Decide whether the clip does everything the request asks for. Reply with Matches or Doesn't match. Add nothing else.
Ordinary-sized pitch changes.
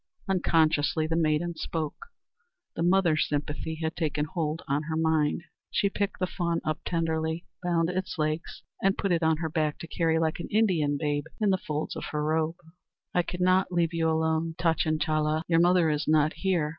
Doesn't match